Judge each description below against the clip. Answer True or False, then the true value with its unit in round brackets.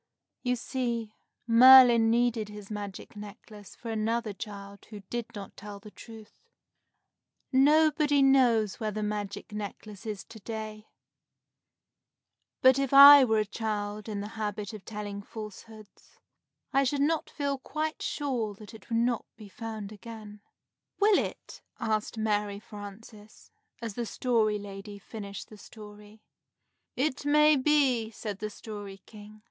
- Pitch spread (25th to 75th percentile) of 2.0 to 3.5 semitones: True (2.8 semitones)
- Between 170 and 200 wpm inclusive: False (140 wpm)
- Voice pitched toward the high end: True (220 Hz)